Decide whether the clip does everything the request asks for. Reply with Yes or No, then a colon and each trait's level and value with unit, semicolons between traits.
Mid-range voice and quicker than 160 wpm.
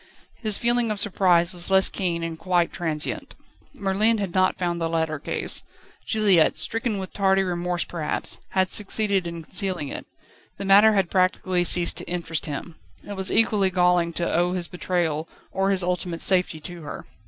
Yes: medium, 180 Hz; average, 175 wpm